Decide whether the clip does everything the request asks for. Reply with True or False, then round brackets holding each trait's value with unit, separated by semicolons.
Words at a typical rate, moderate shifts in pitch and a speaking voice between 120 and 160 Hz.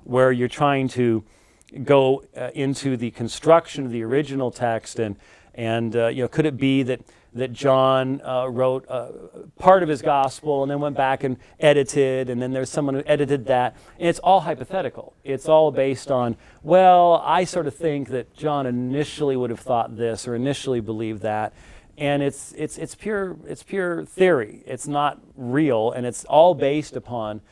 True (185 wpm; 3.3 semitones; 135 Hz)